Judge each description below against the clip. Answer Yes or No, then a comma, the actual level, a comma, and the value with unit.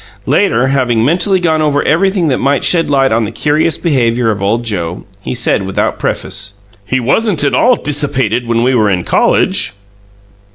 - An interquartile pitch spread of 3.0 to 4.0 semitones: No, average, 5.2 semitones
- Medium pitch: No, low, 130 Hz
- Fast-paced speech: No, average, 175 wpm